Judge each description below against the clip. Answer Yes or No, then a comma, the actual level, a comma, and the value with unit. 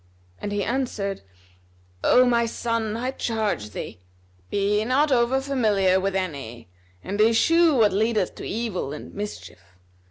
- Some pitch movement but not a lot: Yes, average, 3.5 semitones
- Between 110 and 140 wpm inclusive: Yes, slow, 135 wpm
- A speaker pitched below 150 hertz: No, high, 215 Hz